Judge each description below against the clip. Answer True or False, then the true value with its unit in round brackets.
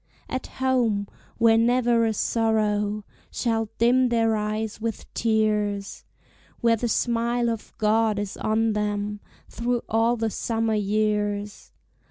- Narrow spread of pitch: True (1.7 semitones)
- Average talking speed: False (125 wpm)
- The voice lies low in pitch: False (220 Hz)